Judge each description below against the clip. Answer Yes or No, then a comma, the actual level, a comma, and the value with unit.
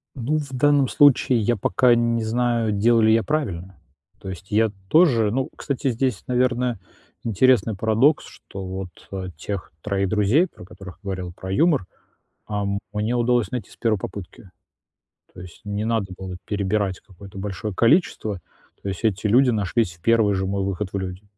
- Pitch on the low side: Yes, low, 110 Hz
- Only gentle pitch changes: No, average, 4.0 semitones